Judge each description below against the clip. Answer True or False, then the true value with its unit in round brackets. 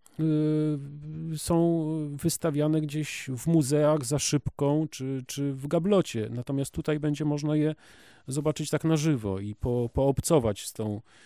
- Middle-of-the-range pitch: True (150 Hz)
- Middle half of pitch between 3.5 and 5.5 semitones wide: False (2.7 semitones)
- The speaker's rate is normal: True (140 wpm)